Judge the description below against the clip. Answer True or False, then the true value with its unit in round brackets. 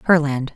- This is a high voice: False (150 Hz)